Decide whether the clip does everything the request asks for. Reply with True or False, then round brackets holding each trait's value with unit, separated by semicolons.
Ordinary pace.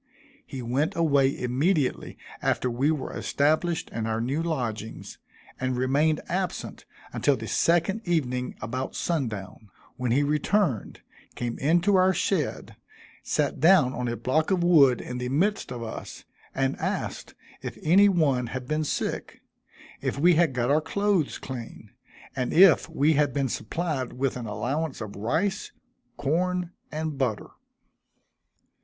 True (145 wpm)